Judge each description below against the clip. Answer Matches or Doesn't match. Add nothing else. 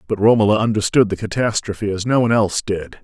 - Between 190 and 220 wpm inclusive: Matches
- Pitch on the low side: Matches